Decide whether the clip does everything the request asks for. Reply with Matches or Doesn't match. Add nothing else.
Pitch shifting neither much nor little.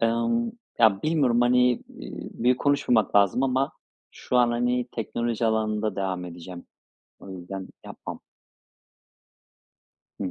Matches